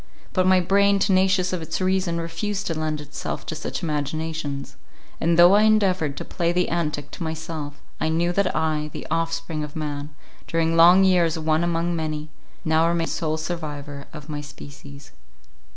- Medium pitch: Yes, medium, 165 Hz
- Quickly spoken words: No, average, 165 wpm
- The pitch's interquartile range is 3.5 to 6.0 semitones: No, narrow, 2.5 semitones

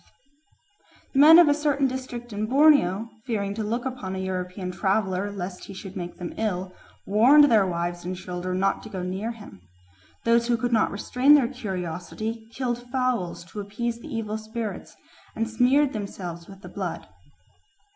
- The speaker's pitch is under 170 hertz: No, high, 215 Hz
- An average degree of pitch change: Yes, average, 4.6 semitones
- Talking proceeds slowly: No, average, 170 wpm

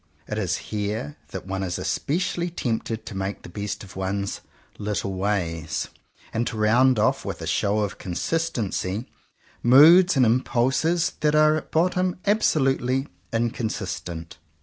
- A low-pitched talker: Yes, low, 110 Hz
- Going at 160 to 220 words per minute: No, average, 150 wpm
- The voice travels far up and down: Yes, wide, 7.2 semitones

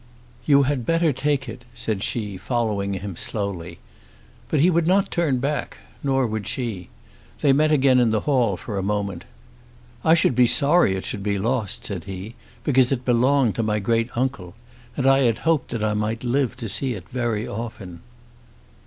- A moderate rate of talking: Yes, average, 185 wpm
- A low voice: Yes, low, 120 Hz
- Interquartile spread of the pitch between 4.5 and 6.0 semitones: Yes, average, 4.8 semitones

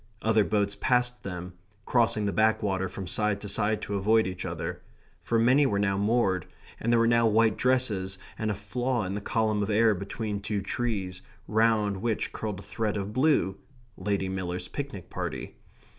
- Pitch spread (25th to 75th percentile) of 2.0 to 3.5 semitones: Yes, narrow, 2.6 semitones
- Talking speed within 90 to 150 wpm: No, average, 180 wpm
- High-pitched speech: No, low, 105 Hz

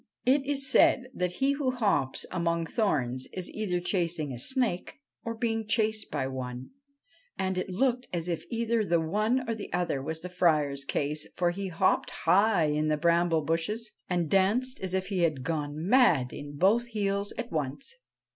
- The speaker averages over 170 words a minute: Yes, average, 180 wpm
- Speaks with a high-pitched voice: No, medium, 180 Hz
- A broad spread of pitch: Yes, wide, 6.0 semitones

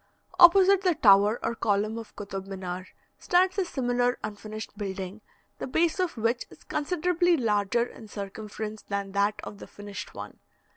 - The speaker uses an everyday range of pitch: No, wide, 7.2 semitones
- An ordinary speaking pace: Yes, average, 155 wpm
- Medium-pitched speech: No, high, 220 Hz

